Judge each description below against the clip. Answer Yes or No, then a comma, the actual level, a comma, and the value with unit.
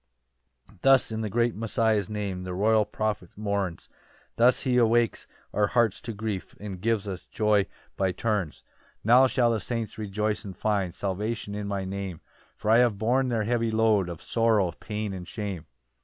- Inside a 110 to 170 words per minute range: No, average, 180 wpm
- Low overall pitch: Yes, low, 105 Hz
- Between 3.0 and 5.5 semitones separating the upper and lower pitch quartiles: No, narrow, 2.6 semitones